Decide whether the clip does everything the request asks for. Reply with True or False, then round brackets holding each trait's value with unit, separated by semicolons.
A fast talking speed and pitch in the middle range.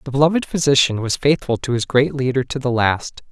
False (215 wpm; 130 Hz)